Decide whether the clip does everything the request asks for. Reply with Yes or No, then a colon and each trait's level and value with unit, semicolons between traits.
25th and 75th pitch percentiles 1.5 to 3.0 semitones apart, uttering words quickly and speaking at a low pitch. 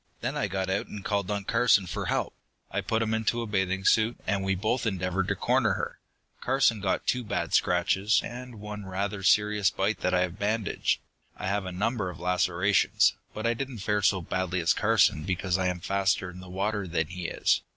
Yes: average, 2.7 semitones; fast, 210 wpm; low, 100 Hz